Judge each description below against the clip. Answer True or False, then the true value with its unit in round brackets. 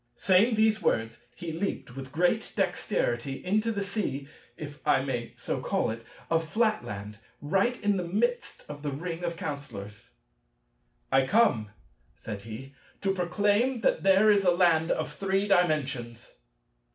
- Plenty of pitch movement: True (6.9 semitones)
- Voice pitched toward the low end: False (170 Hz)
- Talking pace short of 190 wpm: True (150 wpm)